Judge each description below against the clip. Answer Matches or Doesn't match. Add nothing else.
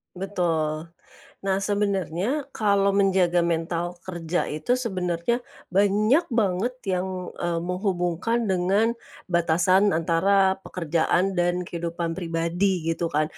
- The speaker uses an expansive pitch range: Doesn't match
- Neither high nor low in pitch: Matches